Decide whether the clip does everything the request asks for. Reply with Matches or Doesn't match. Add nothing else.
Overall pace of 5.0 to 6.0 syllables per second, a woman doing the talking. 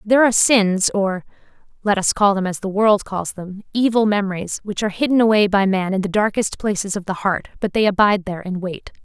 Matches